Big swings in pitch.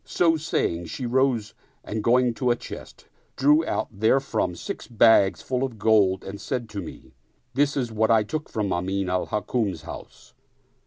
No: average, 4.6 semitones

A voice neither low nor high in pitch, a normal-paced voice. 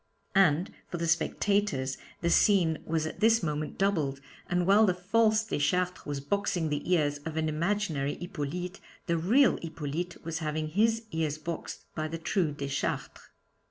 Yes: medium, 165 Hz; average, 160 wpm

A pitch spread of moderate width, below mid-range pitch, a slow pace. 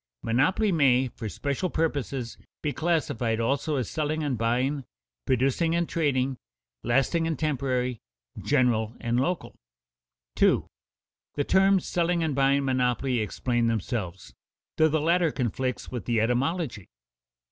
Yes: average, 4.8 semitones; low, 130 Hz; slow, 125 wpm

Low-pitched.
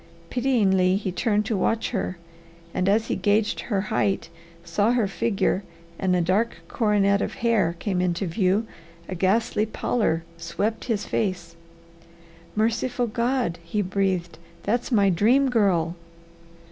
No: high, 205 Hz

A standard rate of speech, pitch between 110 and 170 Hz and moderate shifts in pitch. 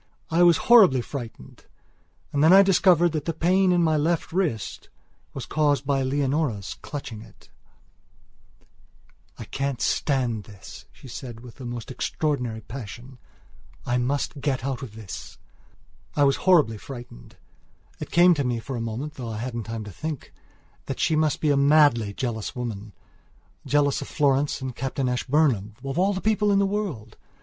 Yes: average, 165 wpm; low, 135 Hz; average, 4.9 semitones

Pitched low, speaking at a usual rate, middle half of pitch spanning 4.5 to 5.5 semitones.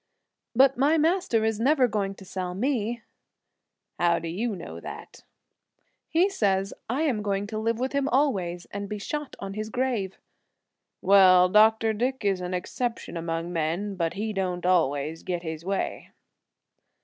No: high, 205 Hz; average, 160 wpm; average, 5.0 semitones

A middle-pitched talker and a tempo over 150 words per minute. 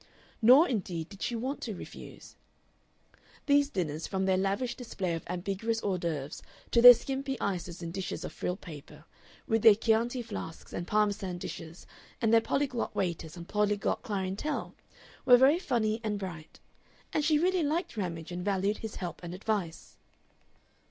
No: high, 205 Hz; average, 160 wpm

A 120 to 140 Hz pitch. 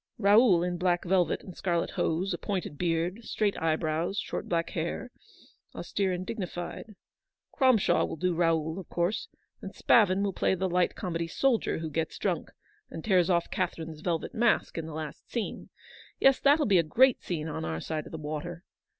No: medium, 175 Hz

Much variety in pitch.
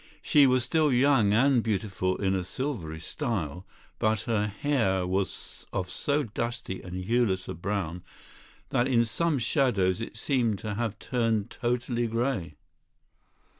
No: average, 4.6 semitones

